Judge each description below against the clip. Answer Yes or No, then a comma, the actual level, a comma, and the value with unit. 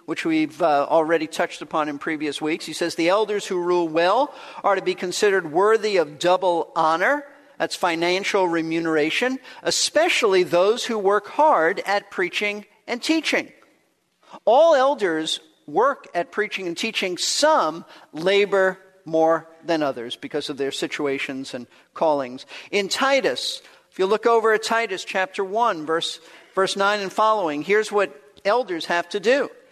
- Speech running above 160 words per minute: No, average, 150 wpm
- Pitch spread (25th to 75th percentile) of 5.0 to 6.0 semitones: Yes, wide, 5.6 semitones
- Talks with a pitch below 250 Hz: Yes, high, 190 Hz